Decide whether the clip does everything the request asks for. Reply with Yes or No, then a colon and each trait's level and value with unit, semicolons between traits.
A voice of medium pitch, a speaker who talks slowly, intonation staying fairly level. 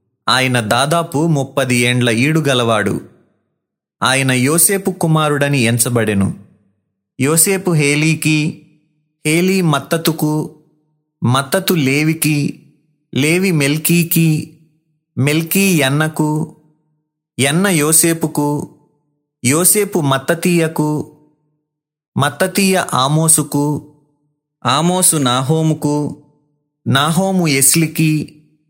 Yes: medium, 150 Hz; slow, 60 wpm; narrow, 2.1 semitones